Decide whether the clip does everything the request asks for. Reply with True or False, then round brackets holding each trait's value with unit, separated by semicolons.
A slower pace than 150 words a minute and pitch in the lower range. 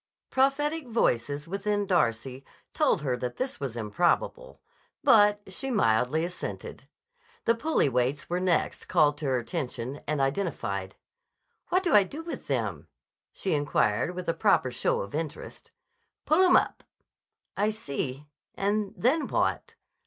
False (140 wpm; 175 Hz)